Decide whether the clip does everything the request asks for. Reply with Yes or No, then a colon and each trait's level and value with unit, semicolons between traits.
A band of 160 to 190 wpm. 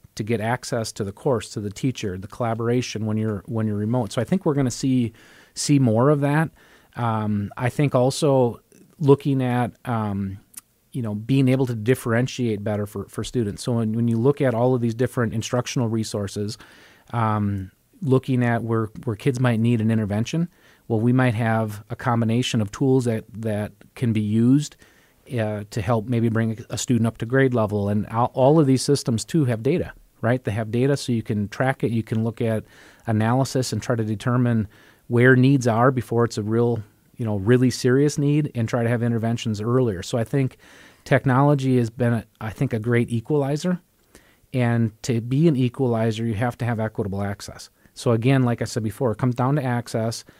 No: average, 200 wpm